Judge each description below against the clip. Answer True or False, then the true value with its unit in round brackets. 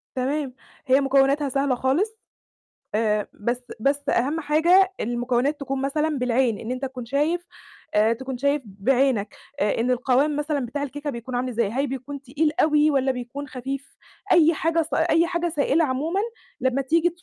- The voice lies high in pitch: True (275 Hz)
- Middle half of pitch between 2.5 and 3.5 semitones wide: True (3.1 semitones)